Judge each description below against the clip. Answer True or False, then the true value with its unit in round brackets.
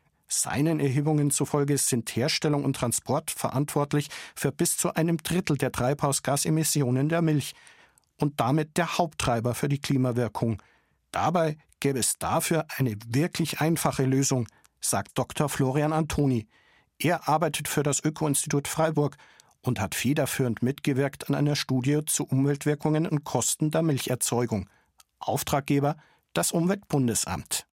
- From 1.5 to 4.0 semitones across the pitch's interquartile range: True (2.8 semitones)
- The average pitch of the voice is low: False (145 Hz)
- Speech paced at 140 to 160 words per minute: False (130 wpm)